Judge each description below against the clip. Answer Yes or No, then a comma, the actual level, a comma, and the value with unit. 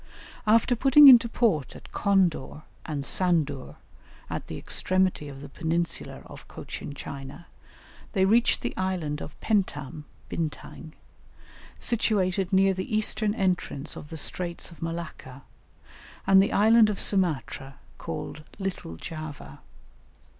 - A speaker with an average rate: No, slow, 125 wpm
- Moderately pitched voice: Yes, medium, 180 Hz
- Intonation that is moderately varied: Yes, average, 4.9 semitones